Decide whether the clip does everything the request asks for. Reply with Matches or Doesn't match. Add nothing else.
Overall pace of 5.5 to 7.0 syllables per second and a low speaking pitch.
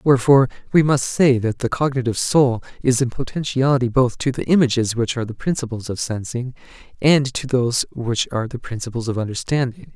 Matches